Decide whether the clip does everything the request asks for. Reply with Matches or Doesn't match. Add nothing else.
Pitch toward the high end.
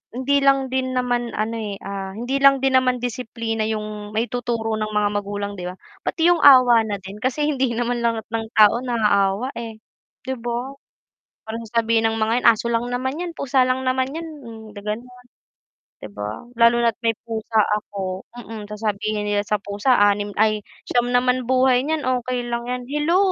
Matches